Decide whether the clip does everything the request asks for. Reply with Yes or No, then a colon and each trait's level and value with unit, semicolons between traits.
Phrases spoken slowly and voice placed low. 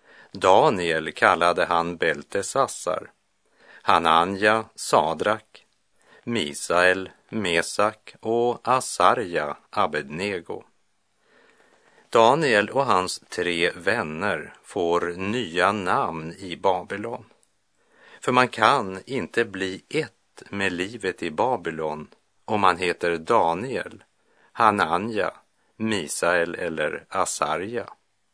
Yes: slow, 85 wpm; very low, 95 Hz